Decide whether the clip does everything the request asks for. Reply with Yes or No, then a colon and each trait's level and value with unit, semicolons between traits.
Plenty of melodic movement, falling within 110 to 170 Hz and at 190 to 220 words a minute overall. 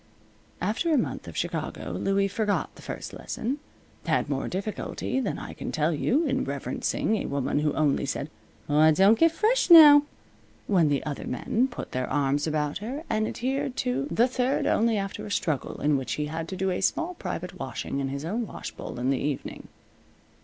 No: wide, 8.9 semitones; high, 190 Hz; average, 195 wpm